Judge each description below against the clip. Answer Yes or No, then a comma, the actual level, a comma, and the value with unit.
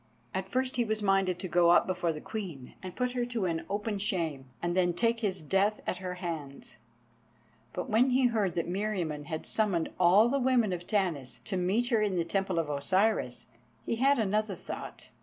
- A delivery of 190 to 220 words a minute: Yes, average, 200 wpm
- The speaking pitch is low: No, high, 190 Hz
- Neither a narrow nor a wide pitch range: Yes, average, 4.1 semitones